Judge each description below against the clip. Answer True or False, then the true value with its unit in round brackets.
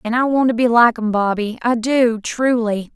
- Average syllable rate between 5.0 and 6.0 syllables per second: False (4.7 syllables/s)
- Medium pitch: False (235 Hz)